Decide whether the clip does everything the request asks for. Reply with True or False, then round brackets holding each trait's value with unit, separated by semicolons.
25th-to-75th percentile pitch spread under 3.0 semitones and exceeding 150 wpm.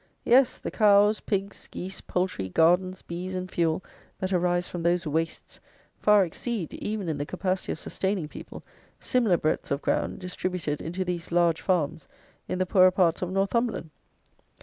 True (2.4 semitones; 160 wpm)